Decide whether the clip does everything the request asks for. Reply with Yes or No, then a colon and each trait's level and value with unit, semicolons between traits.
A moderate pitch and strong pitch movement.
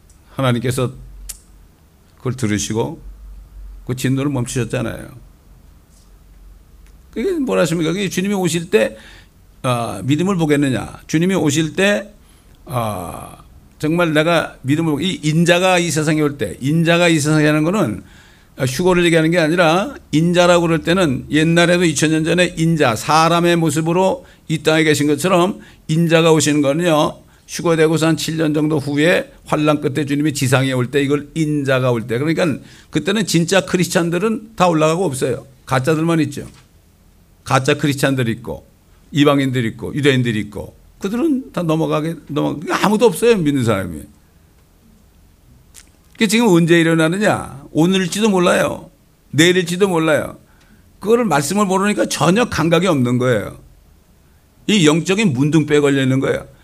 Yes: medium, 150 Hz; wide, 6.1 semitones